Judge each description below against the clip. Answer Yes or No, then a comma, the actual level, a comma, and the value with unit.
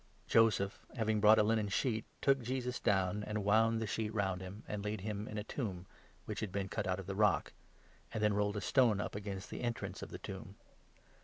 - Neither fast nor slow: No, fast, 225 wpm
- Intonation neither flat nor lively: No, narrow, 1.9 semitones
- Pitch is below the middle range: Yes, low, 105 Hz